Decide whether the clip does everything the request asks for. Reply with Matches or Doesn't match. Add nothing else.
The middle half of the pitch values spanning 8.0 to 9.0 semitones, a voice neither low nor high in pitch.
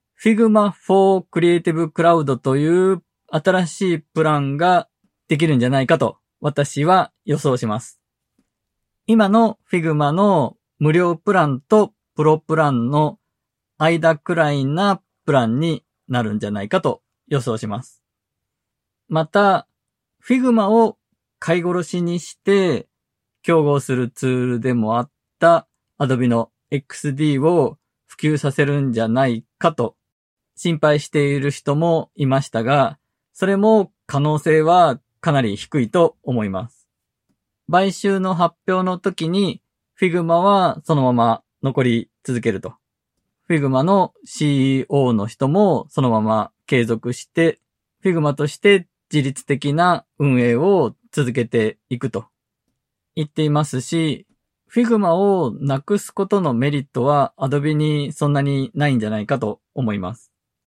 Doesn't match